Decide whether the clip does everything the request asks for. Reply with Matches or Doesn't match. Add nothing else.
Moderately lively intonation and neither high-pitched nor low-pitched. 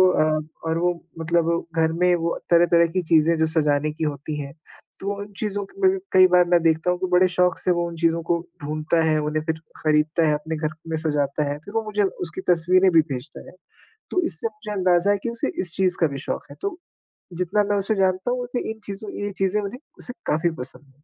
Matches